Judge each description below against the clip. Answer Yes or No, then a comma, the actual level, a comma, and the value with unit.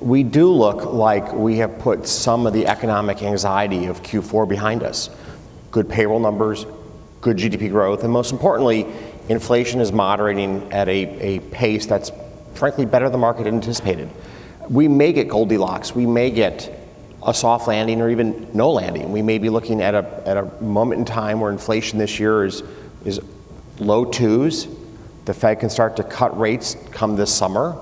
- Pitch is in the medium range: No, low, 110 Hz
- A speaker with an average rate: Yes, average, 175 wpm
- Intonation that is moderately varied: No, narrow, 1.9 semitones